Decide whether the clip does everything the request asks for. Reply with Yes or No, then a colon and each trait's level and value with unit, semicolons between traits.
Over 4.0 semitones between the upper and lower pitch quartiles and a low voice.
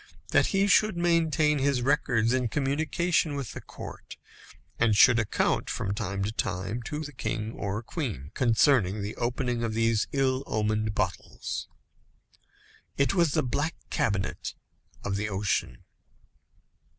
Yes: wide, 5.4 semitones; low, 120 Hz